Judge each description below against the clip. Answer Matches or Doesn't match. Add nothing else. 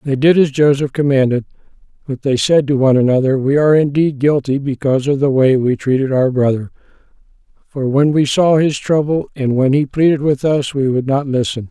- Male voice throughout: Matches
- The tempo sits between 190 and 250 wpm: Matches